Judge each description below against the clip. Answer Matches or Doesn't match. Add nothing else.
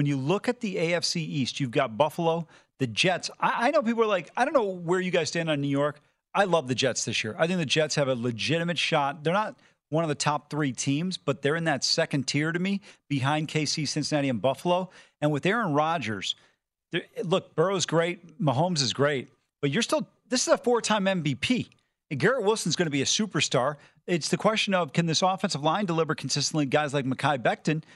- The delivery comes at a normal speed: Doesn't match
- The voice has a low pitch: Doesn't match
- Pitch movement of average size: Matches